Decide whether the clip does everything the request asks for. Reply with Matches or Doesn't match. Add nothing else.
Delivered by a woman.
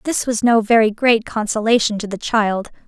Matches